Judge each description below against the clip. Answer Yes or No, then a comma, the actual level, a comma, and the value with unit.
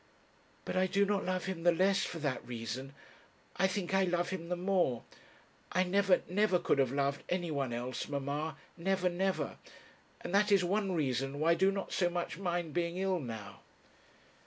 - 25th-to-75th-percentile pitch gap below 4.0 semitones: No, average, 5.0 semitones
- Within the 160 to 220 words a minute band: Yes, average, 185 wpm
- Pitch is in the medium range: Yes, medium, 175 Hz